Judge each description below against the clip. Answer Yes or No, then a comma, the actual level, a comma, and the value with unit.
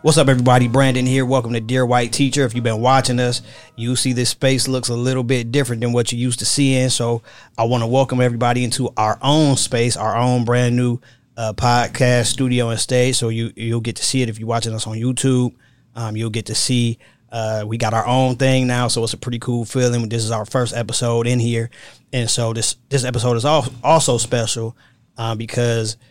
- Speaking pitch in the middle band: No, low, 120 Hz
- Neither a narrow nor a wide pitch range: No, narrow, 1.8 semitones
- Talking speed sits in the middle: No, fast, 225 wpm